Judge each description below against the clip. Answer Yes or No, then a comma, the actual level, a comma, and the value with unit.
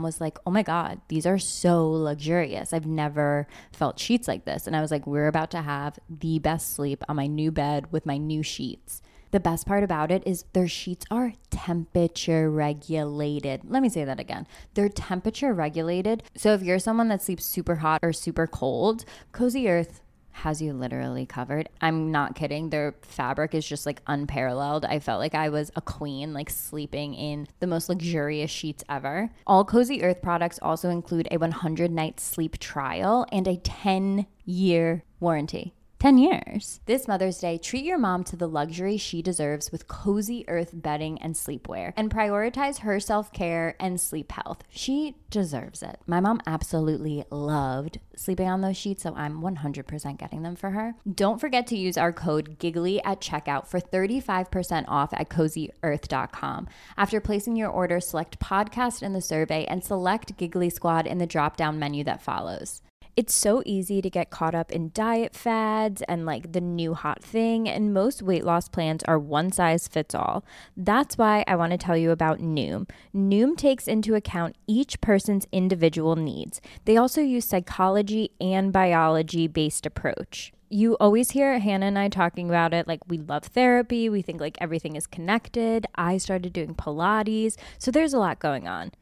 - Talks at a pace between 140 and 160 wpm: No, average, 180 wpm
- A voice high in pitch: No, medium, 175 Hz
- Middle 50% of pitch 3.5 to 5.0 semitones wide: Yes, average, 4.6 semitones